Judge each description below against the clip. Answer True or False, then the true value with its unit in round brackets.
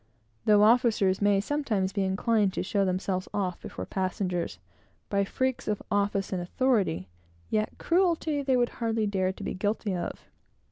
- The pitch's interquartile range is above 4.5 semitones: False (3.5 semitones)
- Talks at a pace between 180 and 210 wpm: False (155 wpm)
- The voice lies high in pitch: True (205 Hz)